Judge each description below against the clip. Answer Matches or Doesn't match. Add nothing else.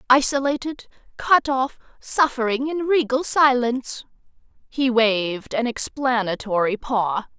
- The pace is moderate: Doesn't match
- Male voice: Doesn't match